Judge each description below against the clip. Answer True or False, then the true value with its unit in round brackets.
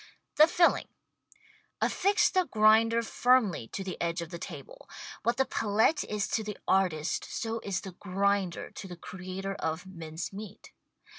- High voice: True (200 Hz)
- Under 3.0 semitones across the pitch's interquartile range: False (3.9 semitones)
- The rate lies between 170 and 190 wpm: False (155 wpm)